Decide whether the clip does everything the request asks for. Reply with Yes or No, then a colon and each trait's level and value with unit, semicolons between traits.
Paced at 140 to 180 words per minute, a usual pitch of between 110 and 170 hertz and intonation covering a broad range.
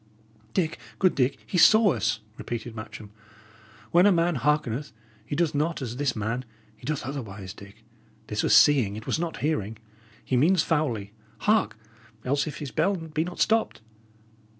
Yes: average, 170 wpm; medium, 140 Hz; wide, 6.6 semitones